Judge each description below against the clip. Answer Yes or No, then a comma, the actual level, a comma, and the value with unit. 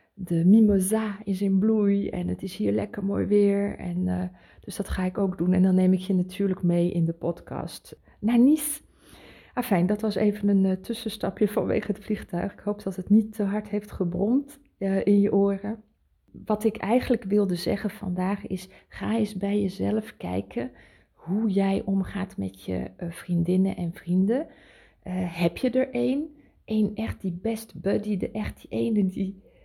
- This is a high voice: Yes, high, 200 Hz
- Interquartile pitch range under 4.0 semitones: Yes, average, 2.7 semitones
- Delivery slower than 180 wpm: No, average, 185 wpm